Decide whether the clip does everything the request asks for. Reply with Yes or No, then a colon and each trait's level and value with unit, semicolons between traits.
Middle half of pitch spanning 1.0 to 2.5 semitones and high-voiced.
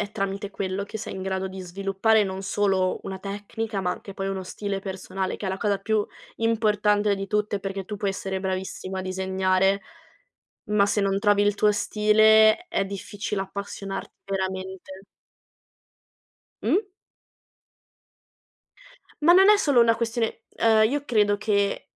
Yes: narrow, 1.8 semitones; high, 200 Hz